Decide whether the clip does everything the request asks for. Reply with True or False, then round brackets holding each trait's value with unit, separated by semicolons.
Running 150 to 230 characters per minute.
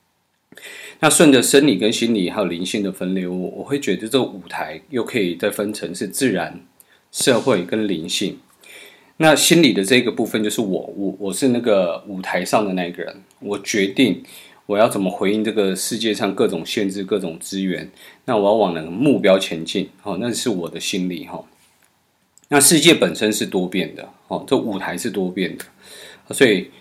False (275 characters per minute)